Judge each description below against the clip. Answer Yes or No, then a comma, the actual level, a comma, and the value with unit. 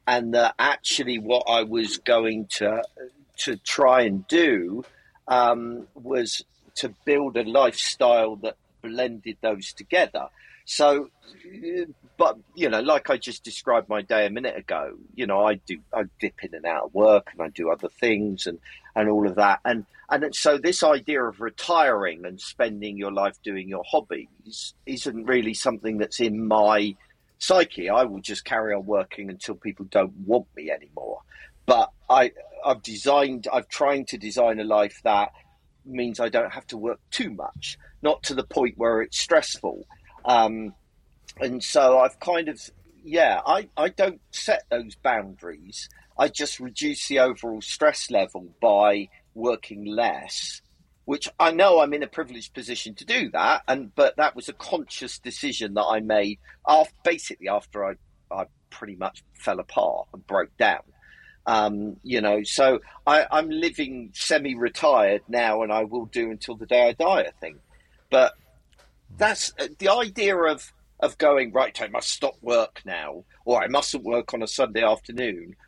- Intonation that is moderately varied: Yes, average, 3.7 semitones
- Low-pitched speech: Yes, low, 115 Hz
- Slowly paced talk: No, average, 170 wpm